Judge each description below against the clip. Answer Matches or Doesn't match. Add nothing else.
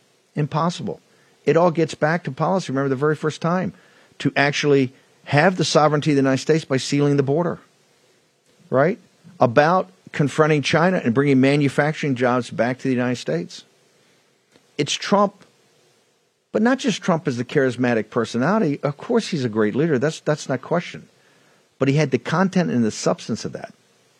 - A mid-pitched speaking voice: Matches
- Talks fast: Doesn't match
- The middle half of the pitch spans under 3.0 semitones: Doesn't match